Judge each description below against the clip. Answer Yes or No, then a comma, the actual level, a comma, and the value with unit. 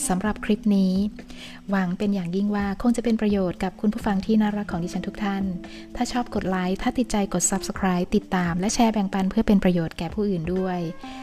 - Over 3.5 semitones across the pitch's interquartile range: No, narrow, 2.4 semitones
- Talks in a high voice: Yes, high, 195 Hz